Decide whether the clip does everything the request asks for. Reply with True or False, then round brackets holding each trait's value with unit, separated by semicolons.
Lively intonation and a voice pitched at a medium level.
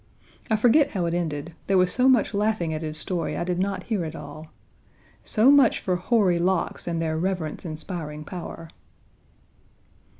False (4.3 semitones; 180 Hz)